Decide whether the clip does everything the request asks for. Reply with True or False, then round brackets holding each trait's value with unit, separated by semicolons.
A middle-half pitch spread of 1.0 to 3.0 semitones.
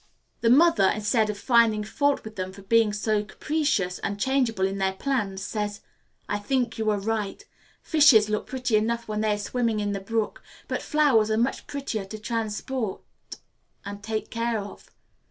True (2.5 semitones)